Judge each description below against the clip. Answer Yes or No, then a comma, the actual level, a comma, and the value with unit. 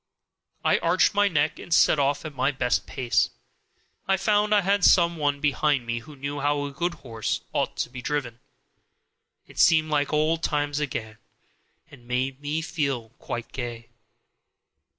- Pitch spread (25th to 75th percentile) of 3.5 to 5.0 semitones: Yes, average, 3.9 semitones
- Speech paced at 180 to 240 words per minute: No, average, 165 wpm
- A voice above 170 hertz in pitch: No, medium, 145 Hz